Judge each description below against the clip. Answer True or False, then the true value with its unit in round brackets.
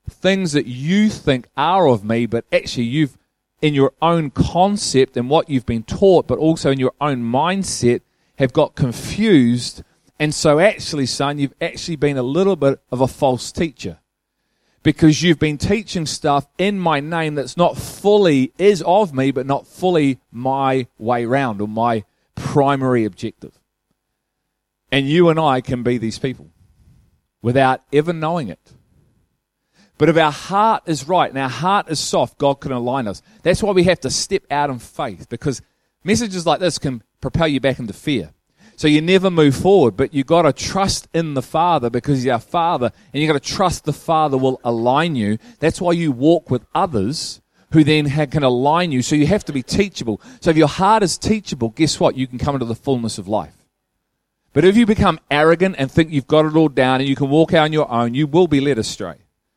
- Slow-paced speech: False (200 wpm)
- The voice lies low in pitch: False (145 Hz)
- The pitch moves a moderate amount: True (4.4 semitones)